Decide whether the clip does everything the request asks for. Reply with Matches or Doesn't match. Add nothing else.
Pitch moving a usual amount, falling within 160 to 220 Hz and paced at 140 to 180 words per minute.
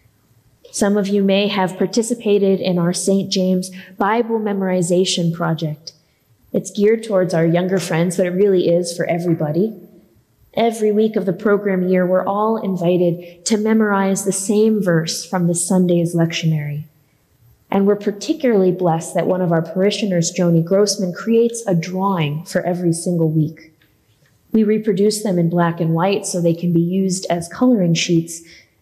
Matches